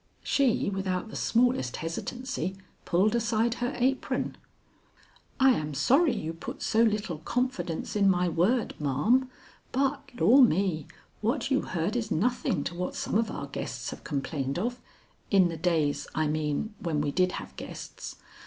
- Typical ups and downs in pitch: No, wide, 7.1 semitones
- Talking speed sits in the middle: Yes, average, 155 wpm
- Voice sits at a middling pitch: No, high, 200 Hz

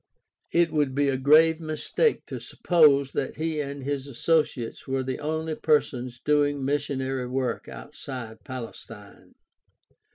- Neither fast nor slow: No, slow, 130 wpm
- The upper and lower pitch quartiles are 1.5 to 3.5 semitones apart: Yes, average, 2.9 semitones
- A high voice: No, medium, 140 Hz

